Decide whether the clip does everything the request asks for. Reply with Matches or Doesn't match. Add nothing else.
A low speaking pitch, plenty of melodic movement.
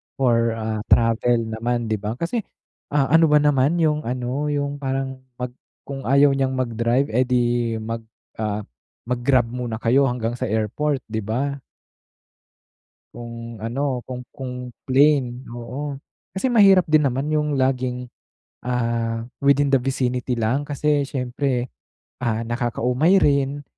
Doesn't match